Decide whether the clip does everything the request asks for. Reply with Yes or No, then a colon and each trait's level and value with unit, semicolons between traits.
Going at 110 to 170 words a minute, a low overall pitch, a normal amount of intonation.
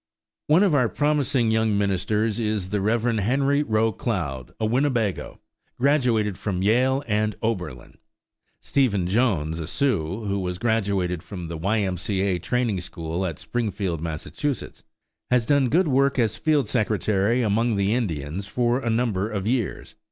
Yes: average, 155 wpm; low, 110 Hz; average, 4.4 semitones